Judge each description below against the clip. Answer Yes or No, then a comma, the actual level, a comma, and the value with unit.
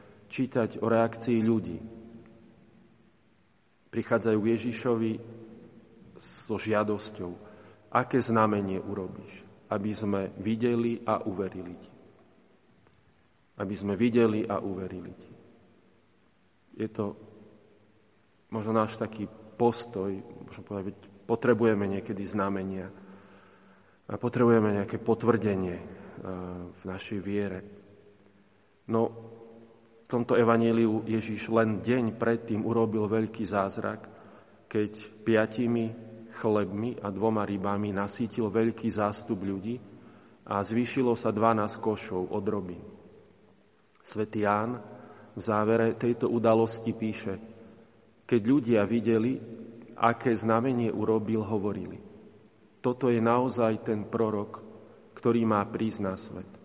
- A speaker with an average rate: No, slow, 100 wpm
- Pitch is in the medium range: No, low, 110 Hz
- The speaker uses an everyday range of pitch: No, narrow, 2.0 semitones